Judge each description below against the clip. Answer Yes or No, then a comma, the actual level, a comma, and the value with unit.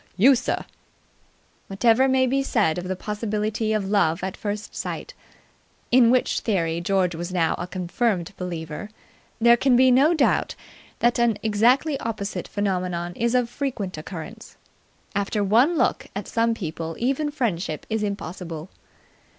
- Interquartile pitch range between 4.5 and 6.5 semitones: Yes, average, 4.8 semitones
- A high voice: Yes, high, 210 Hz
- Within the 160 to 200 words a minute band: No, average, 145 wpm